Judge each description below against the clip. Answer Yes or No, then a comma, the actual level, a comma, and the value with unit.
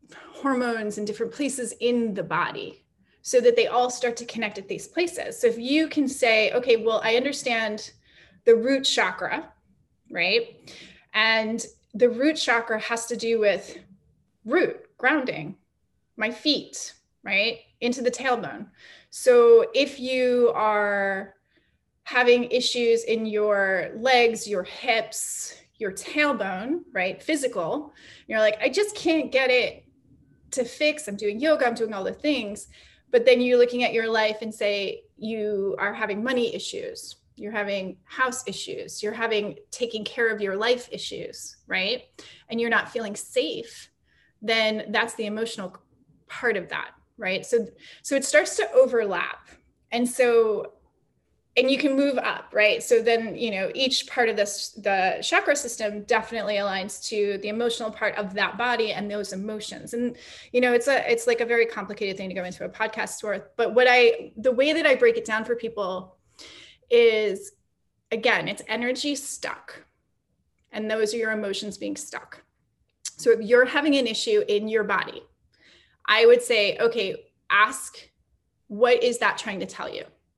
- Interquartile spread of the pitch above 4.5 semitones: Yes, average, 5.3 semitones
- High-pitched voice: Yes, high, 235 Hz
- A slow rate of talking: No, average, 160 wpm